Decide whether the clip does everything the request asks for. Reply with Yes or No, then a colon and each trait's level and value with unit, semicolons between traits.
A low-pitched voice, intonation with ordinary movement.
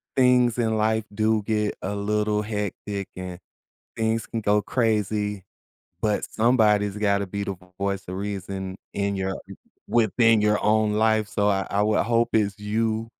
No: low, 105 Hz; narrow, 1.6 semitones